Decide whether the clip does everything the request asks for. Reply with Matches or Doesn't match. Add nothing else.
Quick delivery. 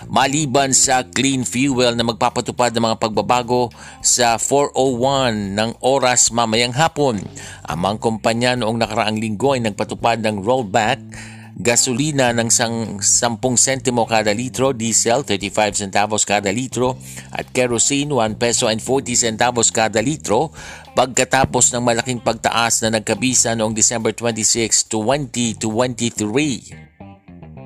Doesn't match